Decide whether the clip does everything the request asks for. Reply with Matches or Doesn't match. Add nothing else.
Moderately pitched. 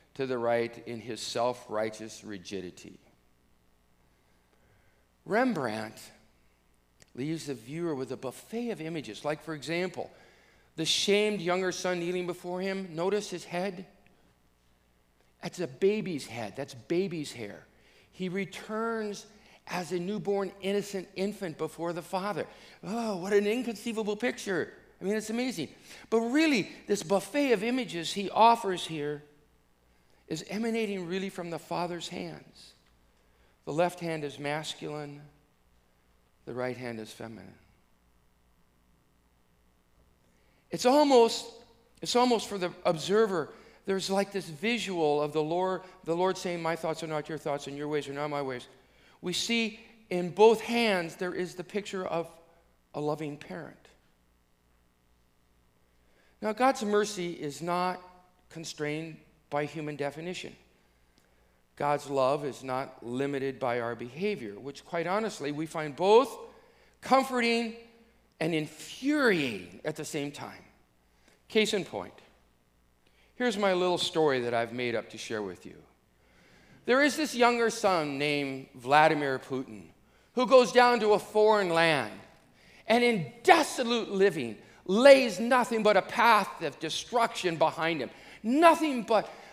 Matches